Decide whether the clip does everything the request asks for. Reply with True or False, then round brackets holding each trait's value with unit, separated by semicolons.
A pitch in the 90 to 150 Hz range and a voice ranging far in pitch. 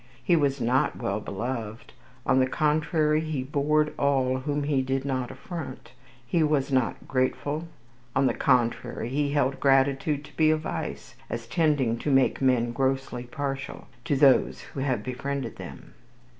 False (135 Hz; 2.4 semitones)